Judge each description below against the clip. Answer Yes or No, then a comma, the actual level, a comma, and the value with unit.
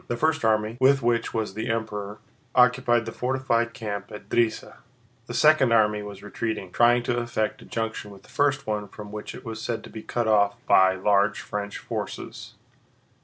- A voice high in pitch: No, low, 110 Hz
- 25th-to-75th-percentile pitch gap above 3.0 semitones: No, narrow, 2.4 semitones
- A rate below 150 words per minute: No, average, 185 wpm